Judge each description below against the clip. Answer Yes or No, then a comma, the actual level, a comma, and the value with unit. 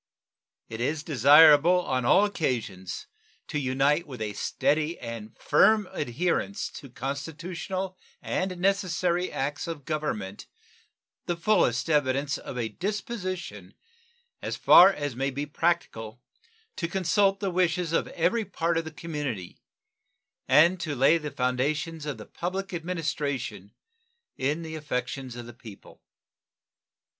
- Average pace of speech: No, slow, 130 wpm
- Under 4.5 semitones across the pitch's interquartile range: No, average, 5.3 semitones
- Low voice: No, medium, 150 Hz